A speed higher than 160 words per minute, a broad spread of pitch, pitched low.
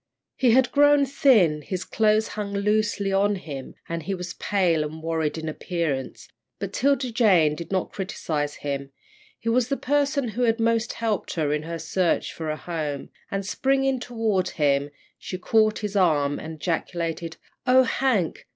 No: average, 170 wpm; wide, 6.2 semitones; high, 190 Hz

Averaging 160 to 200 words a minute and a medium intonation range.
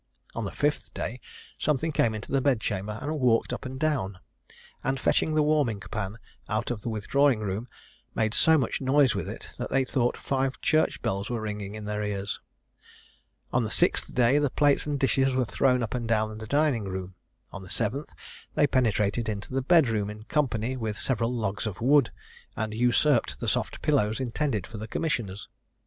Yes: average, 190 wpm; average, 4.3 semitones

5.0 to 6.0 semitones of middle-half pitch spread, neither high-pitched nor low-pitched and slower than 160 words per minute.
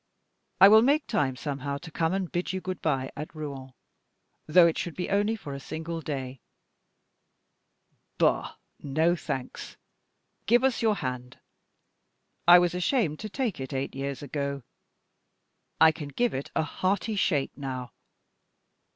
Yes: average, 5.3 semitones; medium, 160 Hz; average, 150 wpm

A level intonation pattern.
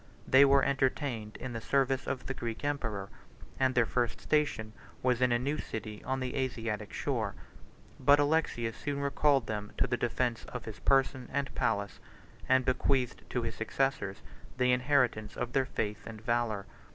No: average, 3.3 semitones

